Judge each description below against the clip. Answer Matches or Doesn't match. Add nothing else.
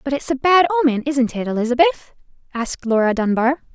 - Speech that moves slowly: Doesn't match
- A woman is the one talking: Matches